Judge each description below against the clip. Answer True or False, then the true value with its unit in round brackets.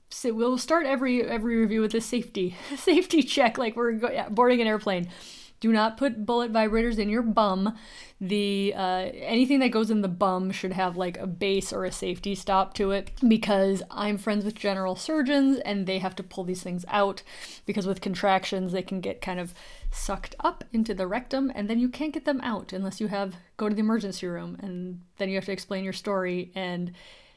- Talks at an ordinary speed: False (210 wpm)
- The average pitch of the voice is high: True (205 Hz)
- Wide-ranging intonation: False (3.7 semitones)